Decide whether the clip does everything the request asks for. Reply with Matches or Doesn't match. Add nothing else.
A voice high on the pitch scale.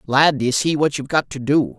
Doesn't match